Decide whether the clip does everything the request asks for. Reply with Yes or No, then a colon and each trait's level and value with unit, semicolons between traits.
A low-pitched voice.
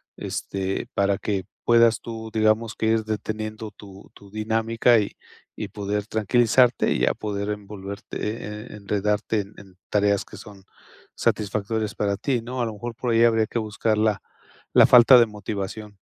Yes: low, 105 Hz